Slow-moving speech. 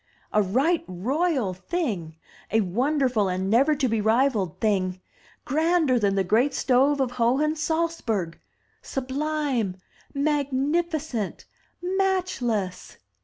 Yes: slow, 110 wpm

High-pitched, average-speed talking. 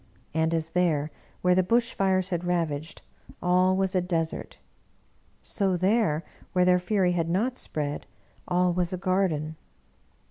No: medium, 180 Hz; average, 150 wpm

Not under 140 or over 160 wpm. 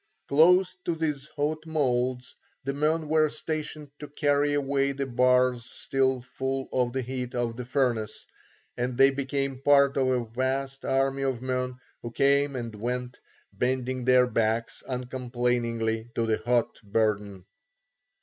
Yes: average, 145 wpm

